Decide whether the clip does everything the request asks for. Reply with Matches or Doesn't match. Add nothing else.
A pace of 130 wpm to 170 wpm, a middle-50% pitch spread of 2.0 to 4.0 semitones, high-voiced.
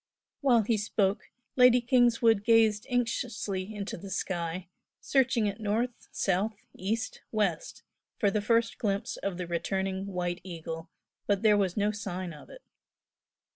Matches